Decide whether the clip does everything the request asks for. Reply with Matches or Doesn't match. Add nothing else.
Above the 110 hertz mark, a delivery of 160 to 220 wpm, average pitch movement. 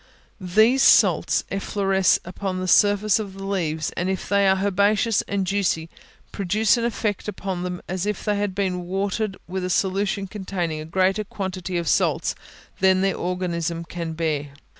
Doesn't match